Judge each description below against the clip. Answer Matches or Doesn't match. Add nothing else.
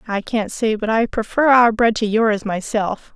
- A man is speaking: Doesn't match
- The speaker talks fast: Matches